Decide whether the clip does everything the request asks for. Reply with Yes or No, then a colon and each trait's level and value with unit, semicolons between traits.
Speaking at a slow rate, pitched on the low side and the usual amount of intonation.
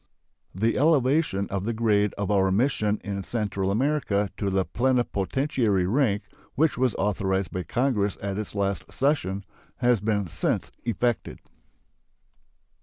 Yes: slow, 130 wpm; low, 105 Hz; average, 4.0 semitones